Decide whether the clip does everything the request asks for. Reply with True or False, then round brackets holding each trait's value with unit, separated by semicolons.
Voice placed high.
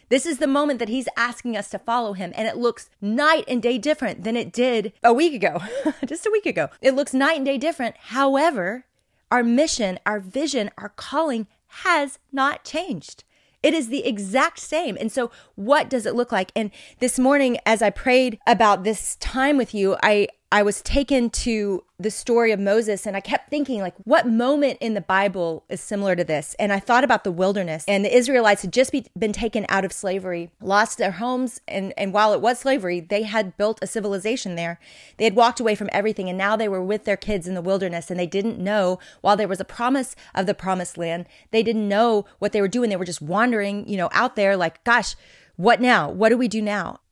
True (220 Hz)